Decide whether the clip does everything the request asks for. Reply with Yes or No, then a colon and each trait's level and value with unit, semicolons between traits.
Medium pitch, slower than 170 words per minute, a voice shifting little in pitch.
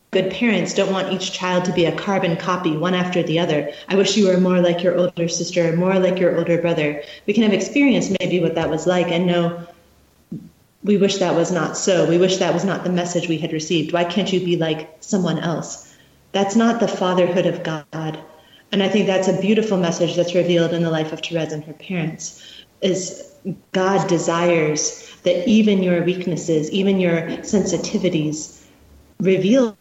No: medium, 175 Hz; average, 195 wpm; narrow, 2.2 semitones